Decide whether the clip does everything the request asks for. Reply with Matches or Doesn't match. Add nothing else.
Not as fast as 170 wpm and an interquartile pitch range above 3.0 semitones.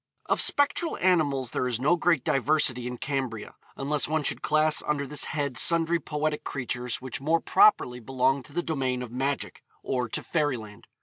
Doesn't match